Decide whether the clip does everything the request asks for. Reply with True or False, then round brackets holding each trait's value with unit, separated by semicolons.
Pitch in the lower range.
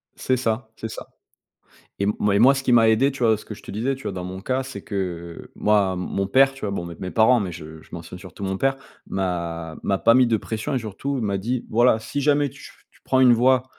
True (110 Hz)